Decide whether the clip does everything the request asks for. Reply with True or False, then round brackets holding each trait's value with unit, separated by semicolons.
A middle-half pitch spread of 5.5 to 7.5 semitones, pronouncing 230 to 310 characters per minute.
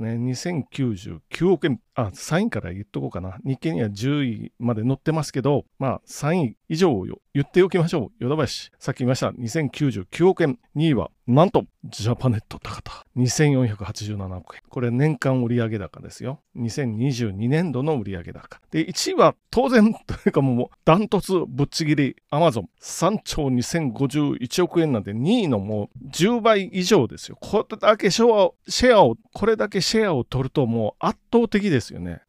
True (6.2 semitones; 295 characters per minute)